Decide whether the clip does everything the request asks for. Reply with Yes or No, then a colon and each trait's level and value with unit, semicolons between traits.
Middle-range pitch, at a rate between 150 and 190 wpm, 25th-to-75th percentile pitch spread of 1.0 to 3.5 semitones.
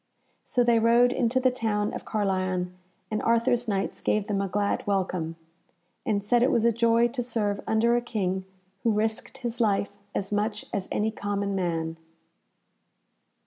No: high, 215 Hz; average, 165 wpm; average, 2.9 semitones